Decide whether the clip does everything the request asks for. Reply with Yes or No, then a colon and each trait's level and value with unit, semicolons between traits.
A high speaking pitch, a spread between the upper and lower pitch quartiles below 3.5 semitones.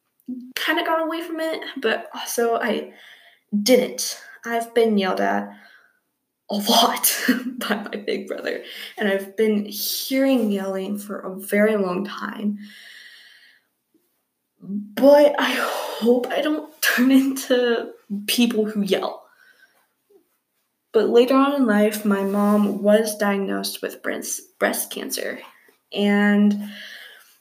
No: high, 230 Hz; average, 4.9 semitones